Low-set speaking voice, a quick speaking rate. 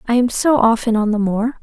No: high, 230 Hz; fast, 260 wpm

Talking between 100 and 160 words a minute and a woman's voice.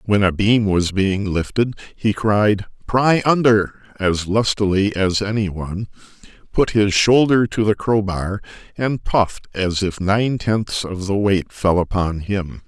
No: average, 155 wpm; male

